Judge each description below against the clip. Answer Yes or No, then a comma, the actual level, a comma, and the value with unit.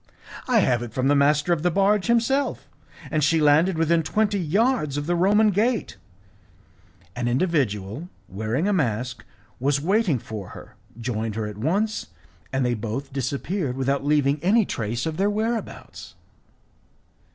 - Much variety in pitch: Yes, wide, 7.6 semitones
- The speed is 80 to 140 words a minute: No, average, 150 wpm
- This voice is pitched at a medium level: Yes, medium, 150 Hz